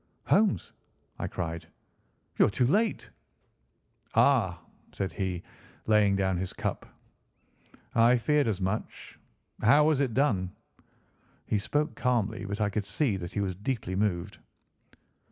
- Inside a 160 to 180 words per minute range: No, slow, 135 wpm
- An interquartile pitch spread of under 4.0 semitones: No, average, 4.9 semitones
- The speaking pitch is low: Yes, low, 105 Hz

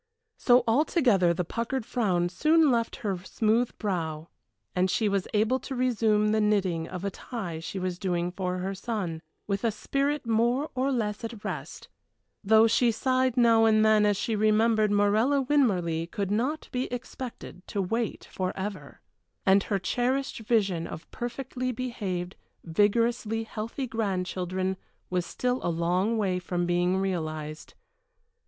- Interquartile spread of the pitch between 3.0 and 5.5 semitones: Yes, average, 4.6 semitones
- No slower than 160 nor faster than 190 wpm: No, average, 150 wpm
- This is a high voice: Yes, high, 210 Hz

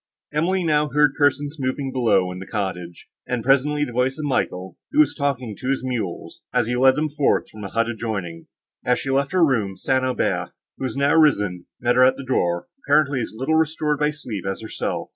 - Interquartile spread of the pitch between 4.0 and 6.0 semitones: Yes, average, 5.1 semitones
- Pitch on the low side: Yes, low, 130 Hz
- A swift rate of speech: Yes, fast, 215 wpm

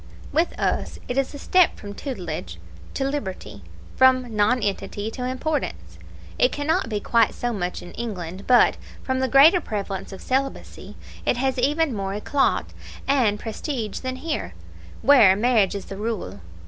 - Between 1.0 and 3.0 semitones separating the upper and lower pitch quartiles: No, average, 5.2 semitones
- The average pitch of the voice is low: No, high, 240 Hz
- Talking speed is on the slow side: No, average, 160 wpm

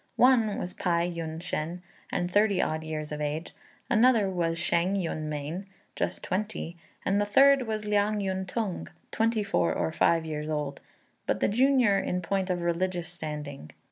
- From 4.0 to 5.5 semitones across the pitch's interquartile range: Yes, average, 4.3 semitones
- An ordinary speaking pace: Yes, average, 170 wpm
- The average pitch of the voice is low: No, medium, 180 Hz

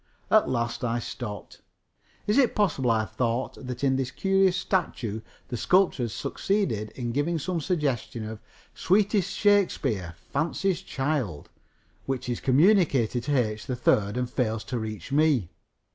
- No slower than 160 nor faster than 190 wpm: No, average, 145 wpm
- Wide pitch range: Yes, wide, 7.1 semitones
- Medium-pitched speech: No, low, 130 Hz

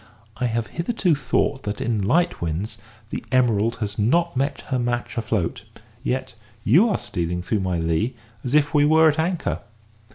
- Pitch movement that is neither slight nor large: No, wide, 6.4 semitones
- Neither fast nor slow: Yes, average, 165 wpm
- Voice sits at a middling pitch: No, low, 120 Hz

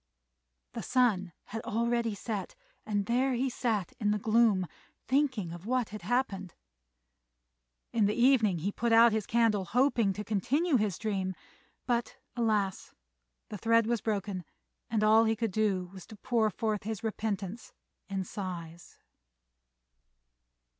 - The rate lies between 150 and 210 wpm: No, average, 140 wpm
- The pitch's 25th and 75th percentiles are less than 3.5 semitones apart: Yes, average, 3.1 semitones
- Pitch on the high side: Yes, high, 215 Hz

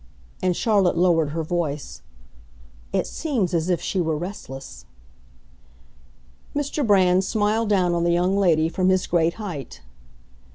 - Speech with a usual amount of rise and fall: Yes, average, 3.4 semitones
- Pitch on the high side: No, medium, 180 Hz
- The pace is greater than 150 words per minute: No, slow, 135 wpm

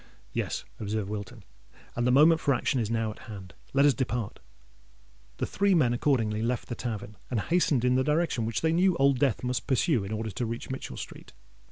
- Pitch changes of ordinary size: Yes, average, 4.2 semitones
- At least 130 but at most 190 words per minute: No, fast, 205 wpm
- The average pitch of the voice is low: Yes, low, 125 Hz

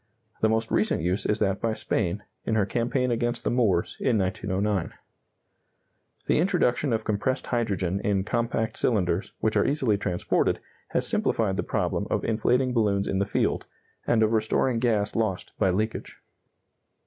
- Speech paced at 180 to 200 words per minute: No, average, 160 wpm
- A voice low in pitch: Yes, low, 110 Hz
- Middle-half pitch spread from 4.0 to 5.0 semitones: No, average, 3.0 semitones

